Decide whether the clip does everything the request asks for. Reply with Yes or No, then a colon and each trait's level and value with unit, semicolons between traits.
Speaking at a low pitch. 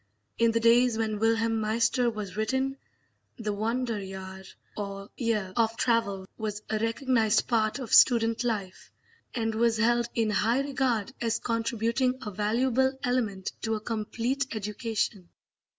No: high, 225 Hz